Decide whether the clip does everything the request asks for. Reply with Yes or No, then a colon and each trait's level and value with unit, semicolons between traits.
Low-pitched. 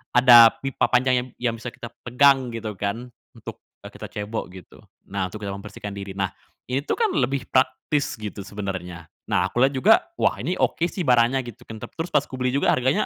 Yes: low, 120 Hz